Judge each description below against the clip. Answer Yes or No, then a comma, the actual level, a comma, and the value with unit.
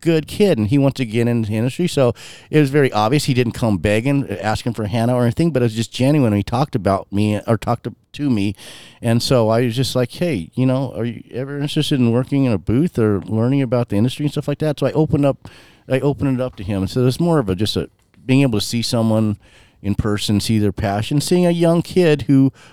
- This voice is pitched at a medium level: No, low, 125 Hz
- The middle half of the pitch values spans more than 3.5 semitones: Yes, average, 4.6 semitones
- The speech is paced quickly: Yes, fast, 255 wpm